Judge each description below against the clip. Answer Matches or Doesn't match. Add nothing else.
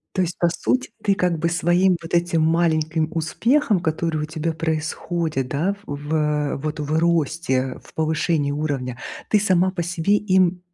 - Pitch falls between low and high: Matches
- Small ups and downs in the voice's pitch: Matches